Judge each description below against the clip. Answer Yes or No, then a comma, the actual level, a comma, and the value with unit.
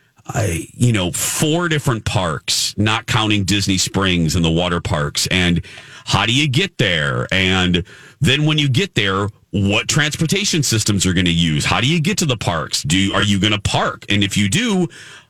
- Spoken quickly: No, average, 190 wpm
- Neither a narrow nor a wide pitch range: No, wide, 7.3 semitones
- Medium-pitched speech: No, low, 105 Hz